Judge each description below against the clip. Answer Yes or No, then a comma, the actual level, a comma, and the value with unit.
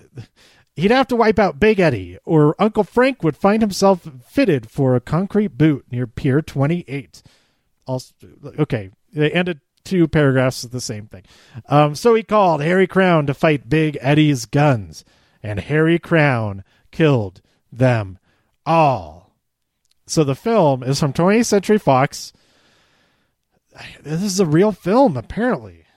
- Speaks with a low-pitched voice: No, medium, 150 Hz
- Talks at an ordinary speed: Yes, average, 145 wpm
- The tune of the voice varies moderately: No, wide, 6.5 semitones